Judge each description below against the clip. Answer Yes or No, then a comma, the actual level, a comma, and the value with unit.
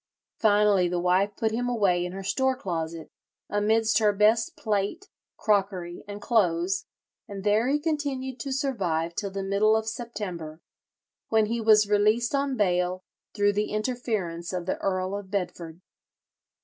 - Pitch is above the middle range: Yes, high, 205 Hz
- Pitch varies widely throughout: No, average, 3.4 semitones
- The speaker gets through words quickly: No, average, 150 wpm